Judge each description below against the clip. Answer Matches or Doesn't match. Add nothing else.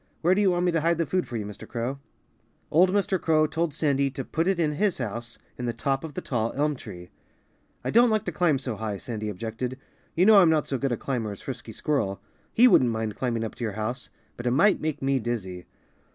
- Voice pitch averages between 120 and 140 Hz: Matches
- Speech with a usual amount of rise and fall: Doesn't match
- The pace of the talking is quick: Matches